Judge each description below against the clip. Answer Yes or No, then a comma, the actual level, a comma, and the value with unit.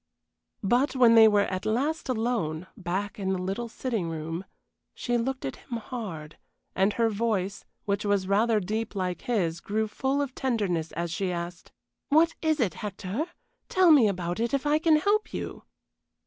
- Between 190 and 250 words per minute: No, average, 175 wpm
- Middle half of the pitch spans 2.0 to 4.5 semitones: No, average, 5.2 semitones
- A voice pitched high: Yes, high, 215 Hz